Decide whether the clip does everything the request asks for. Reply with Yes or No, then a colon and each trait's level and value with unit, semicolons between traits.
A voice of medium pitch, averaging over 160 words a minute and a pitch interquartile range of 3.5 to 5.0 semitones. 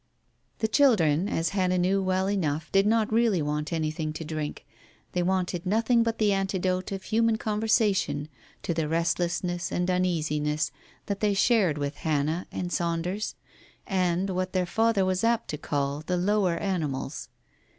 No: medium, 180 Hz; average, 155 wpm; average, 3.9 semitones